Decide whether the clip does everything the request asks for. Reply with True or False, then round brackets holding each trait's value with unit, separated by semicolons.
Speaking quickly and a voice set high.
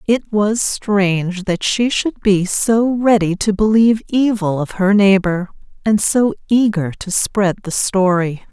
False (155 wpm; 205 Hz)